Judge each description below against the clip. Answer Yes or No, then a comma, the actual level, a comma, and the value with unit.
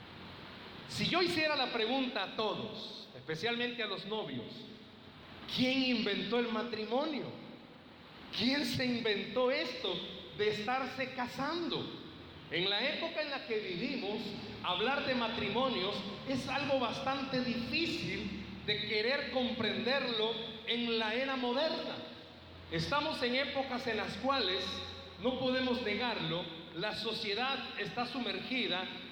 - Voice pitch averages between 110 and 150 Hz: No, high, 245 Hz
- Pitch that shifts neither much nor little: Yes, average, 3.5 semitones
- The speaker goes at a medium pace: No, slow, 115 wpm